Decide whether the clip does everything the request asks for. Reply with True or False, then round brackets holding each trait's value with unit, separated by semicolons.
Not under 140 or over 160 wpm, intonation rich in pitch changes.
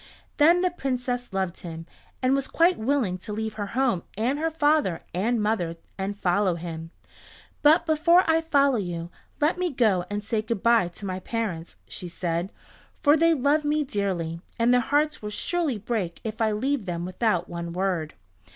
False (180 wpm; 7.9 semitones)